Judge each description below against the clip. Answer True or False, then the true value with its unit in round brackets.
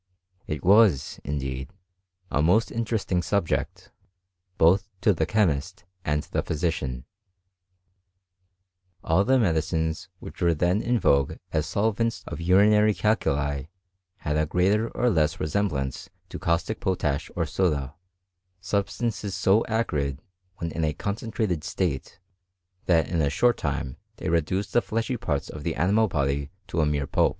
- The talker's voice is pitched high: False (85 Hz)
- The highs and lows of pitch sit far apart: True (5.9 semitones)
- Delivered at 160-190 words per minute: False (145 wpm)